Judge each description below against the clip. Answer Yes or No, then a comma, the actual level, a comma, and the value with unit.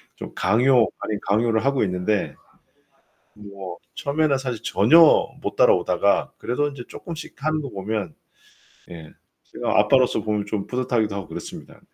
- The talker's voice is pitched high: No, low, 110 Hz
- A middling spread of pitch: Yes, average, 4.9 semitones